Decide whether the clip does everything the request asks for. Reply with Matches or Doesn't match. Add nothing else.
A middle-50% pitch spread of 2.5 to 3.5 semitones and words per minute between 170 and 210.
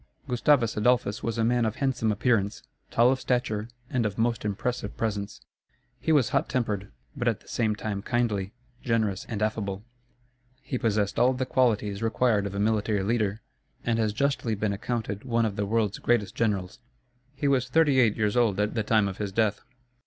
Matches